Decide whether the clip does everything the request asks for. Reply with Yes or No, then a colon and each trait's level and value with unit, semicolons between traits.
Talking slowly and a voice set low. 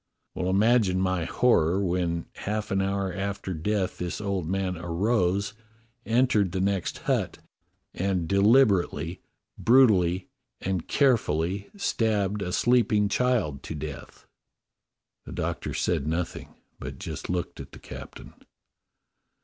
Yes: slow, 120 wpm; very low, 95 Hz